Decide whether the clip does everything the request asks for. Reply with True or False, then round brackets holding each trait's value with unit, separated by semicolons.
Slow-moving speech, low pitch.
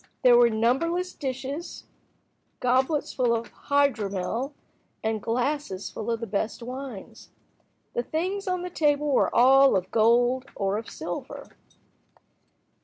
False (125 wpm; 250 Hz)